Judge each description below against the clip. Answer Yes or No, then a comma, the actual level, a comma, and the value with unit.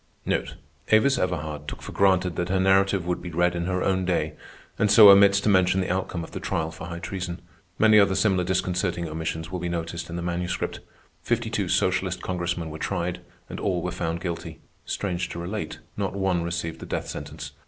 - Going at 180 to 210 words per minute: Yes, average, 200 wpm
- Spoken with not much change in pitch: Yes, narrow, 2.0 semitones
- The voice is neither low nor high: No, very low, 90 Hz